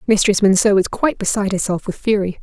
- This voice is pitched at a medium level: No, high, 200 Hz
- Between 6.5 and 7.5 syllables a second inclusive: Yes, 6.6 syllables/s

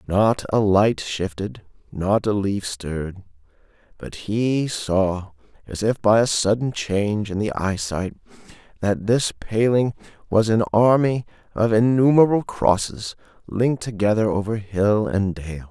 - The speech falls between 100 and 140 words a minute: Yes, slow, 135 wpm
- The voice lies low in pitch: Yes, low, 105 Hz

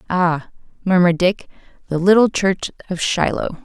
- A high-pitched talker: No, medium, 180 Hz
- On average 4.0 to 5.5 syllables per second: Yes, 5.1 syllables/s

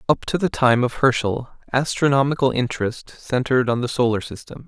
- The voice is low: Yes, low, 125 Hz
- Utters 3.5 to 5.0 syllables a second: No, 5.4 syllables/s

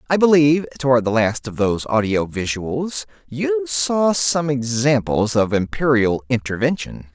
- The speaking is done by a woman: No, male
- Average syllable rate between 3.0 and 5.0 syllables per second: Yes, 4.5 syllables/s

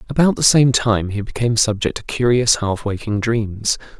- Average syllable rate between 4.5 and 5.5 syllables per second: Yes, 5.0 syllables/s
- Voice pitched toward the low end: Yes, low, 115 Hz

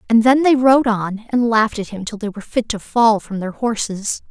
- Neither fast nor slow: No, fast, 250 wpm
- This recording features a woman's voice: Yes, female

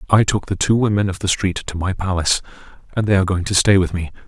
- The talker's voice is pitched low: Yes, very low, 95 Hz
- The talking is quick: Yes, fast, 265 wpm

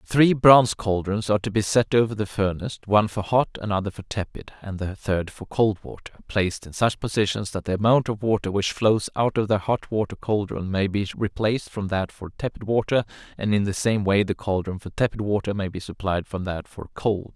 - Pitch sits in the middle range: No, low, 105 Hz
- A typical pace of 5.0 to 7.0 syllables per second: Yes, 5.6 syllables/s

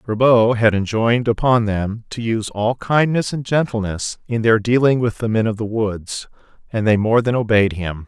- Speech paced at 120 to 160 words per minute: No, average, 195 wpm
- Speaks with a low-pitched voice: Yes, low, 115 Hz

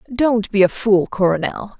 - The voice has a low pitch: No, high, 205 Hz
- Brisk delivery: No, average, 165 wpm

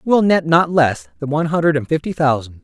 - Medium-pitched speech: Yes, medium, 150 Hz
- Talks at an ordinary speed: No, fast, 230 wpm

